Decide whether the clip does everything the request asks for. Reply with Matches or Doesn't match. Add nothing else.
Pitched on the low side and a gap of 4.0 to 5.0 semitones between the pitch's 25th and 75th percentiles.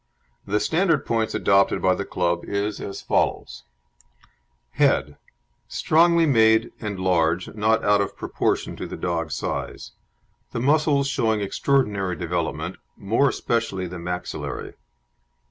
Matches